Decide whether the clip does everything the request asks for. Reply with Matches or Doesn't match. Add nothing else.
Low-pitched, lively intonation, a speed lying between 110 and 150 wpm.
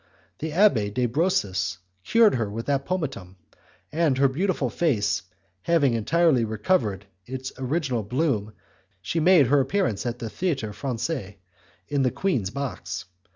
Matches